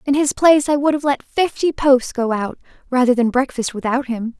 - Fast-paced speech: Yes, fast, 220 wpm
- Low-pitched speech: No, very high, 265 Hz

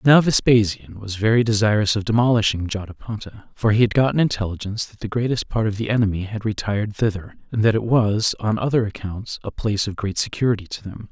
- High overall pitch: No, low, 110 Hz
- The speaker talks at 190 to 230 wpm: Yes, average, 200 wpm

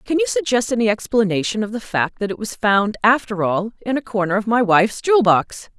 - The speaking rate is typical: No, fast, 230 wpm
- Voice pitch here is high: Yes, high, 215 Hz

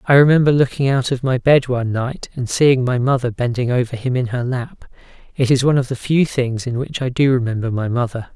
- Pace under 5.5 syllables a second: No, 5.7 syllables/s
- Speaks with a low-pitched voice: Yes, low, 125 Hz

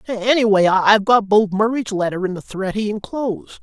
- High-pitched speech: Yes, high, 200 Hz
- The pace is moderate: Yes, average, 180 wpm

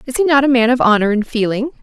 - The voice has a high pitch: Yes, high, 245 Hz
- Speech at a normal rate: No, fast, 295 wpm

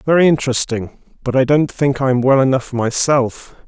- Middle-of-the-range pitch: No, low, 130 Hz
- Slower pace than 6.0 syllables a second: Yes, 5.0 syllables/s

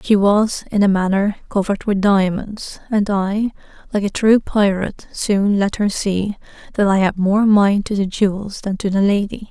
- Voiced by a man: No, female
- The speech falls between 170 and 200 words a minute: Yes, average, 190 wpm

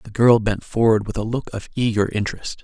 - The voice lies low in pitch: Yes, low, 110 Hz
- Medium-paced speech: No, fast, 230 wpm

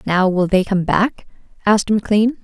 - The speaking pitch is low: No, high, 200 Hz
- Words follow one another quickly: No, average, 175 wpm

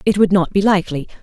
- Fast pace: Yes, fast, 245 wpm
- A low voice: No, high, 190 Hz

